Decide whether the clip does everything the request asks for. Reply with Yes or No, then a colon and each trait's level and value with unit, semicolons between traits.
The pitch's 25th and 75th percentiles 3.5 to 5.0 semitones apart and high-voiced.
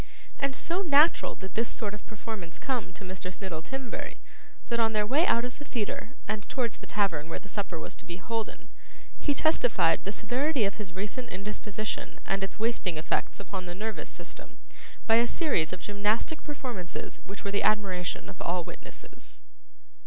Yes: average, 4.2 semitones; high, 210 Hz